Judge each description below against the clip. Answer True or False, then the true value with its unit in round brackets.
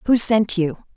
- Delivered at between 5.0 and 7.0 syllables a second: False (4.6 syllables/s)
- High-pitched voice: True (205 Hz)